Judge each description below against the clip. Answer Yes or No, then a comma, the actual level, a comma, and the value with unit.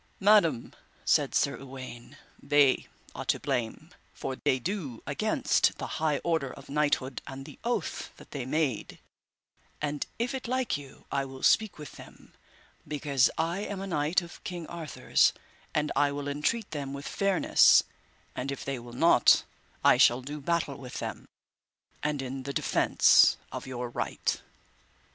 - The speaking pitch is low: No, medium, 145 Hz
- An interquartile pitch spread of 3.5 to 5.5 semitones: Yes, average, 4.0 semitones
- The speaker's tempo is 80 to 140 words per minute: No, average, 160 wpm